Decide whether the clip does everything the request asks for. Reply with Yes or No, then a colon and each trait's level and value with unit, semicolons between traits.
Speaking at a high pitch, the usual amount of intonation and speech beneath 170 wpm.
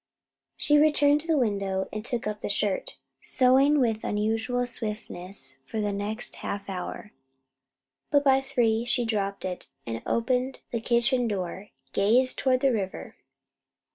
Yes: high, 225 Hz; average, 4.0 semitones; average, 145 wpm